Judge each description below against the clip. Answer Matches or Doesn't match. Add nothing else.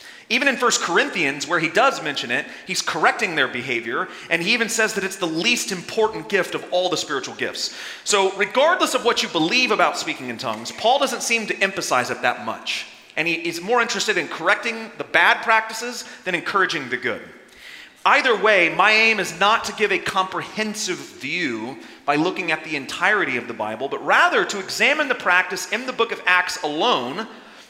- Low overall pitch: Doesn't match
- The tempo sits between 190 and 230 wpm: Matches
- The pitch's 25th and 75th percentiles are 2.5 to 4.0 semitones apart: Doesn't match